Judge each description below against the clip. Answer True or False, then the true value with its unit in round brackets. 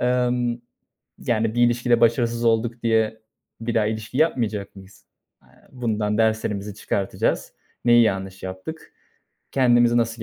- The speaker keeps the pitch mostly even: True (2.0 semitones)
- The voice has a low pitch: True (115 Hz)